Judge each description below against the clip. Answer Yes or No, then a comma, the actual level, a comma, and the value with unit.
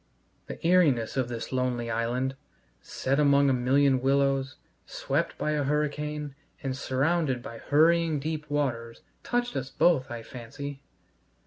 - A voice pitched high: No, low, 135 Hz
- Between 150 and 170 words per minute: No, slow, 135 wpm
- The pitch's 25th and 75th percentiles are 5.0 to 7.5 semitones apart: No, average, 2.8 semitones